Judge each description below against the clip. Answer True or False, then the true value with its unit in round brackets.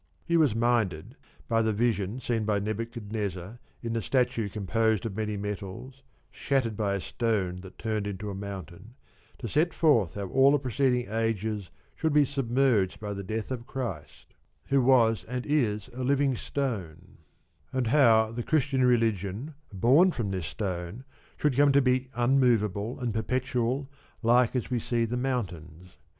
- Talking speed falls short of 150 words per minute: False (160 wpm)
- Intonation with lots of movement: False (4.0 semitones)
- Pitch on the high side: False (115 Hz)